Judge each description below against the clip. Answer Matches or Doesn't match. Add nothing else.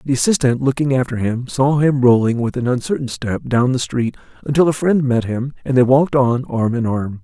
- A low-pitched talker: Matches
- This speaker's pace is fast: Matches